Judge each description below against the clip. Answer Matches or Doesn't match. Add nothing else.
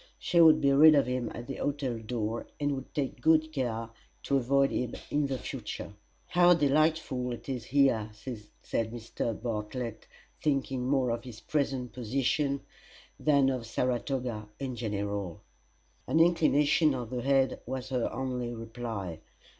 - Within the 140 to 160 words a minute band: Matches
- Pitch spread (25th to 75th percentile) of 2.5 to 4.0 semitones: Matches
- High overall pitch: Doesn't match